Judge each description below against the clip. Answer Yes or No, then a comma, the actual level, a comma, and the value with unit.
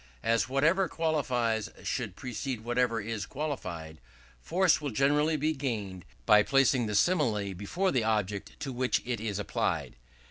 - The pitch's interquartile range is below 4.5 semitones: No, wide, 5.5 semitones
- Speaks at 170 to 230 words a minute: No, average, 145 wpm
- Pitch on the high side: No, low, 125 Hz